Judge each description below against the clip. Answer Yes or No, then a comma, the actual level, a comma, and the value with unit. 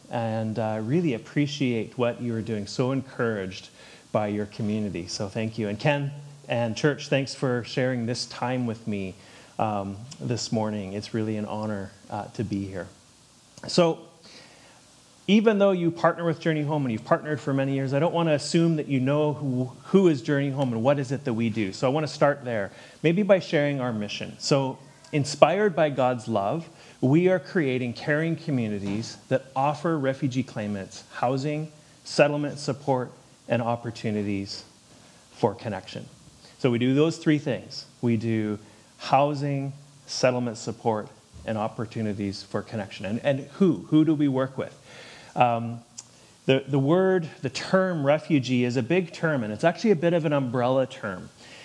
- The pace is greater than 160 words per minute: Yes, average, 170 wpm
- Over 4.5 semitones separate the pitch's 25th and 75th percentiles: Yes, average, 5.0 semitones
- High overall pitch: No, low, 130 Hz